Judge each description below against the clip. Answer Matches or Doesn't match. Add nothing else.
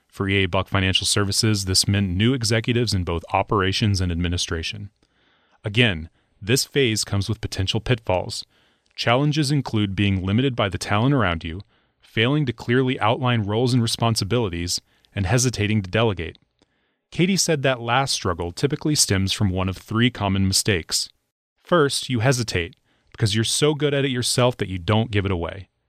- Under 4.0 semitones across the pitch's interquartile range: Doesn't match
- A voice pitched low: Matches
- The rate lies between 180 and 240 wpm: Doesn't match